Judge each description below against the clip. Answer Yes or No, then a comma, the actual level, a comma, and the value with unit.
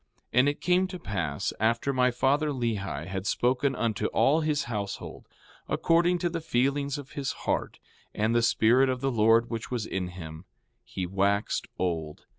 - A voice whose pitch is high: No, low, 120 Hz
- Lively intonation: Yes, wide, 5.9 semitones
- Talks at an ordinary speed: Yes, average, 175 wpm